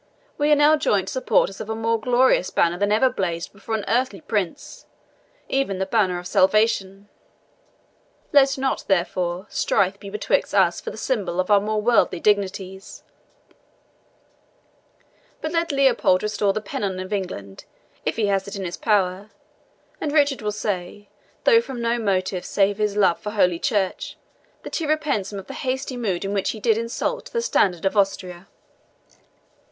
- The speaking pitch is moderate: No, high, 205 Hz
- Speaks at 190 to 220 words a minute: No, average, 170 wpm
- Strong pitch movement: No, average, 4.0 semitones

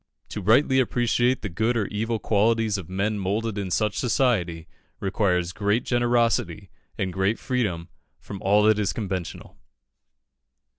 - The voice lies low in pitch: Yes, low, 105 Hz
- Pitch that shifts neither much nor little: Yes, average, 3.3 semitones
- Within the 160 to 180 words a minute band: No, average, 140 wpm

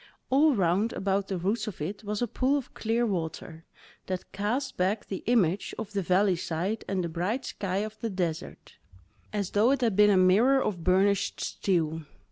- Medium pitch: No, high, 200 Hz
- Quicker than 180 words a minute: Yes, average, 190 wpm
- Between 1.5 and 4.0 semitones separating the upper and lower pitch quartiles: Yes, average, 3.3 semitones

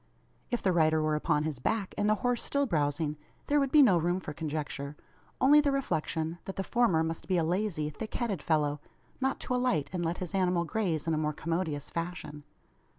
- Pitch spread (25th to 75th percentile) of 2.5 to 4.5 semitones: No, wide, 5.6 semitones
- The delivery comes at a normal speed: No, fast, 210 wpm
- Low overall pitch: No, medium, 170 Hz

